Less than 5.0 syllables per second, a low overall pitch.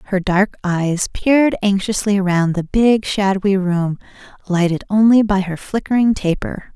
No: 4.6 syllables/s; high, 195 Hz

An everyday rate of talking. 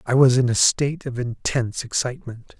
Yes: average, 185 wpm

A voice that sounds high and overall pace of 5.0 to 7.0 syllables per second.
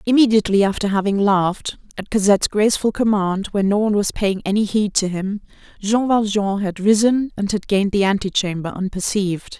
Yes: high, 205 Hz; 5.7 syllables/s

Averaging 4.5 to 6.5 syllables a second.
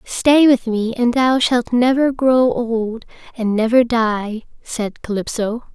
No: 3.6 syllables/s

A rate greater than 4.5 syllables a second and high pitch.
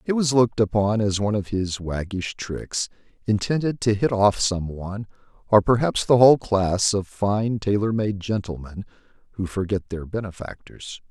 No: 4.8 syllables/s; low, 105 Hz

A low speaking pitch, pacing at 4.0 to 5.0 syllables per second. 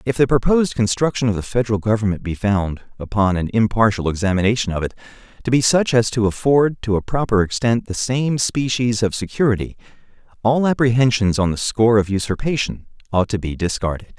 No: low, 110 Hz; 5.9 syllables/s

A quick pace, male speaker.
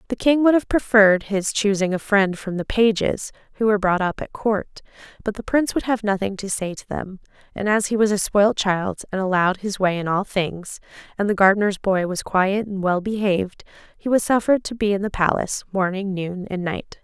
No: fast, 220 wpm; female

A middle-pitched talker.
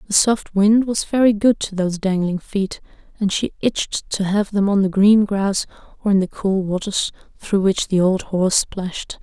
No: high, 200 Hz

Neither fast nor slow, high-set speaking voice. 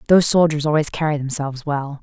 No: average, 175 wpm; medium, 150 Hz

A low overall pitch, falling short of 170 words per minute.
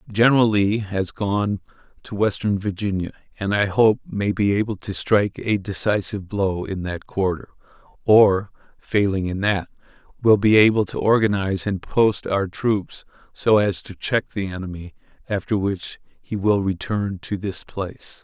Yes: low, 100 Hz; average, 160 wpm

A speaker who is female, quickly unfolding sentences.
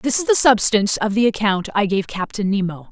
Yes: female; fast, 225 wpm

